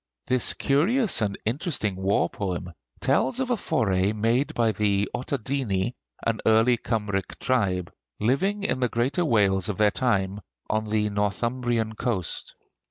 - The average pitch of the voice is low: Yes, low, 110 Hz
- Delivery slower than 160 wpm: Yes, average, 140 wpm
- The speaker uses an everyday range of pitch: Yes, average, 4.1 semitones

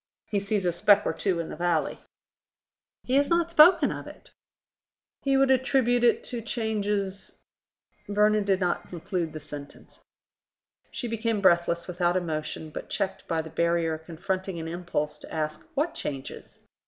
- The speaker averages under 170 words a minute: Yes, average, 160 wpm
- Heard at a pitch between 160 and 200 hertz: Yes, high, 190 Hz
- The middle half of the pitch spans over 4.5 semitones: Yes, average, 5.2 semitones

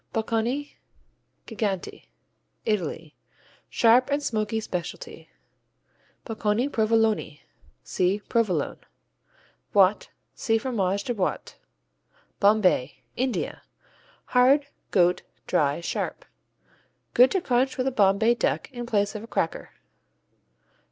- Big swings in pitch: No, average, 4.1 semitones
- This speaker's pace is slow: Yes, slow, 100 wpm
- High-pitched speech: Yes, high, 220 Hz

